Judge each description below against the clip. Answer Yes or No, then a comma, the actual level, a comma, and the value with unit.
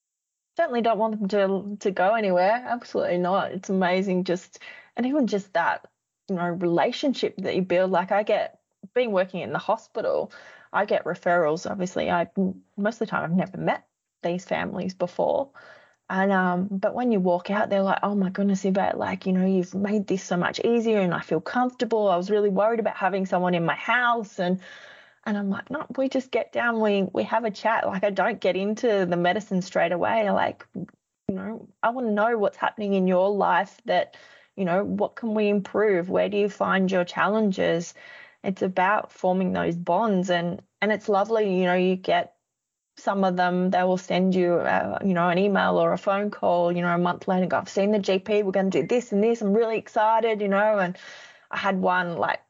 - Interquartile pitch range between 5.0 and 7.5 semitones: No, average, 3.3 semitones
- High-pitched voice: Yes, high, 200 Hz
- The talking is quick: Yes, fast, 215 wpm